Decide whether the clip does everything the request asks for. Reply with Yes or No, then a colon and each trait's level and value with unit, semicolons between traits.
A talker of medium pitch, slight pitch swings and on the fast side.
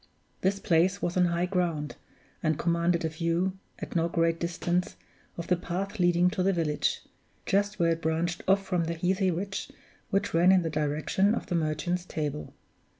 No: medium, 175 Hz; narrow, 2.0 semitones; average, 180 wpm